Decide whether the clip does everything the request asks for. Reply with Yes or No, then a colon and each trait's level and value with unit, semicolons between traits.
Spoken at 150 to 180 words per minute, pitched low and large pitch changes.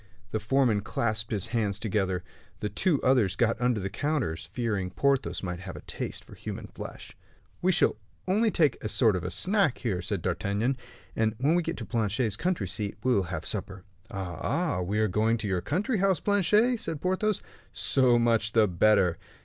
No: average, 190 wpm; low, 110 Hz; wide, 6.4 semitones